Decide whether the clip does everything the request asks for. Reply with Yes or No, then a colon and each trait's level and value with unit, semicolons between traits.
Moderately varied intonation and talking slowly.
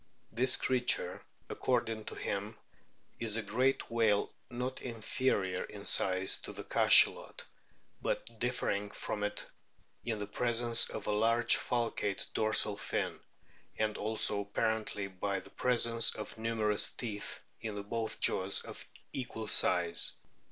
No: narrow, 2.3 semitones; slow, 130 wpm